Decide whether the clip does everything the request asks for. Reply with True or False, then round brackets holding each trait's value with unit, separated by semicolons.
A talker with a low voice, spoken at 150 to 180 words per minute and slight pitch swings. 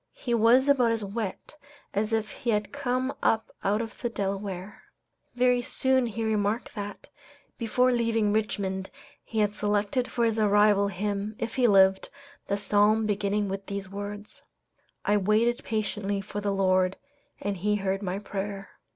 False (210 Hz; 160 wpm; 2.3 semitones)